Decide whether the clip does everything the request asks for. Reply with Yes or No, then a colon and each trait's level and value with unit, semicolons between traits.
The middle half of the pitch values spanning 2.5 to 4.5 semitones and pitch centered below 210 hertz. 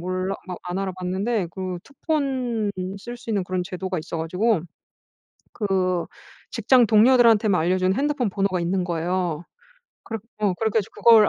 Yes: average, 3.7 semitones; high, 195 Hz